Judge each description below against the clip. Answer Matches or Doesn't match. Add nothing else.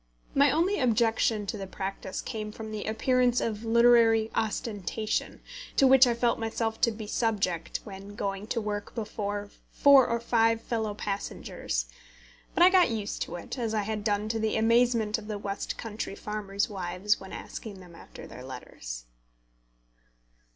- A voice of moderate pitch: Doesn't match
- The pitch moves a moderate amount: Doesn't match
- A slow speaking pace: Doesn't match